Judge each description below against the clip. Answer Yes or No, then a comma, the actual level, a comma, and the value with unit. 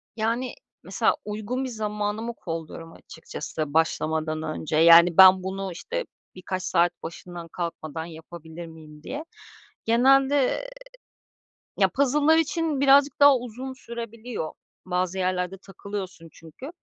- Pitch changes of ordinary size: No, wide, 7.0 semitones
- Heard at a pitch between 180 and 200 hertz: Yes, high, 190 Hz